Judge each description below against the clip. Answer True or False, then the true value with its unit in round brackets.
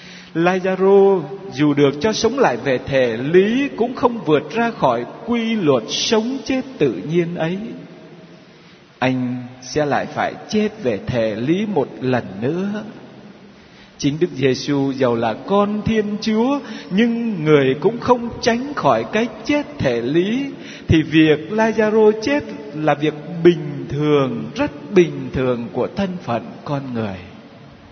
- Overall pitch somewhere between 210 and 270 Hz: False (185 Hz)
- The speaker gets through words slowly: True (140 wpm)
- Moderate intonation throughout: False (7.4 semitones)